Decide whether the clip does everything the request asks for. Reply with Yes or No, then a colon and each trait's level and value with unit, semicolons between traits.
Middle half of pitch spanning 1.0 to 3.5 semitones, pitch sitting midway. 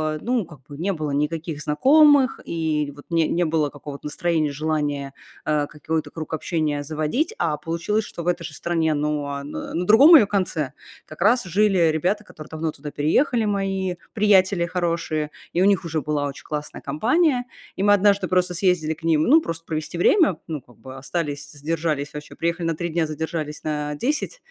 No: average, 4.0 semitones; medium, 160 Hz